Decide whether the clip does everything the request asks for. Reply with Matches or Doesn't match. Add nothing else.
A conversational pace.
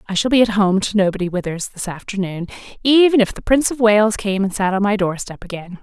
Doesn't match